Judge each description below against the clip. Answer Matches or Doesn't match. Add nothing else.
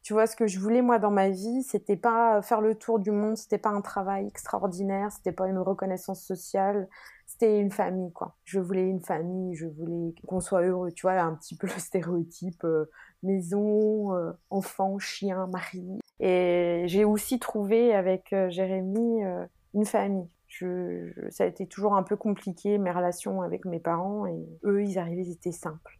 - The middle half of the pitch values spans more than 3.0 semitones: Doesn't match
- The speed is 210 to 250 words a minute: Doesn't match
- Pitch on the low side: Doesn't match